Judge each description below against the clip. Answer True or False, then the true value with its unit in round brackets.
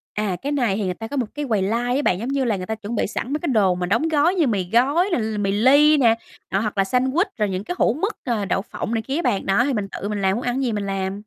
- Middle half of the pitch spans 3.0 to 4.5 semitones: False (5.3 semitones)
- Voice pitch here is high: True (225 Hz)